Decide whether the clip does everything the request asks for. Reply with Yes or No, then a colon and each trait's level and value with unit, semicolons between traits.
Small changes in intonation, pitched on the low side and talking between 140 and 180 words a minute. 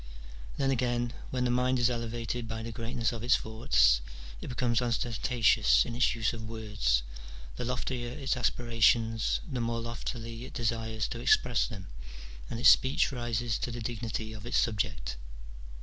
Yes: narrow, 1.6 semitones; low, 115 Hz; average, 165 wpm